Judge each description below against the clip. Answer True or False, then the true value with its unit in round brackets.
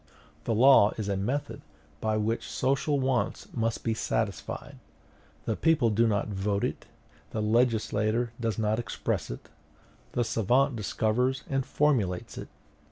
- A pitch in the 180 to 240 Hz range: False (115 Hz)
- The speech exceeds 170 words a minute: False (140 wpm)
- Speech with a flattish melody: False (3.2 semitones)